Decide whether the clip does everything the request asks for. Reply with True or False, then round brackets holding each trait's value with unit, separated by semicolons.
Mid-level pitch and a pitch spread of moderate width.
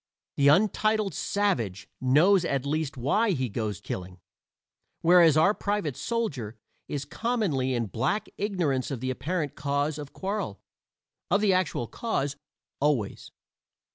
False (150 Hz; 7.3 semitones)